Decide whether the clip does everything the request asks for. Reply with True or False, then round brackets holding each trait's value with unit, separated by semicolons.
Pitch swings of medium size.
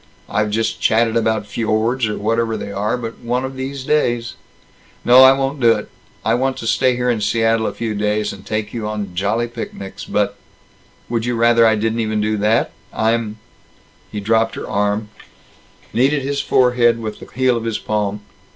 False (2.1 semitones)